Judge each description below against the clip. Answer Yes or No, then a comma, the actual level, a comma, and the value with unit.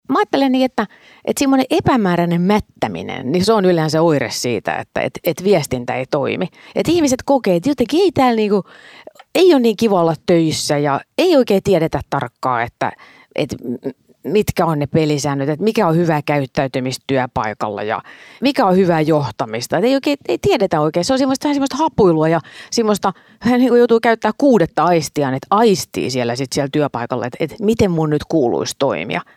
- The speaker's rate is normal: No, fast, 180 wpm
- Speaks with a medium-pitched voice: Yes, medium, 180 Hz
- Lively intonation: Yes, wide, 8.3 semitones